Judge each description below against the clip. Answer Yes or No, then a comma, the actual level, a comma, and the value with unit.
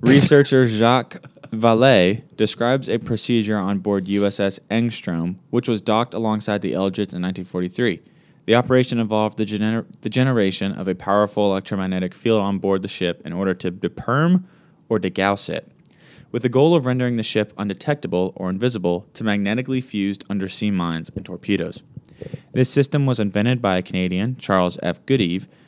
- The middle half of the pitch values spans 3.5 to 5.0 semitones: Yes, average, 4.3 semitones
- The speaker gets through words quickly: No, average, 160 wpm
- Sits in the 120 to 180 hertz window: No, low, 105 Hz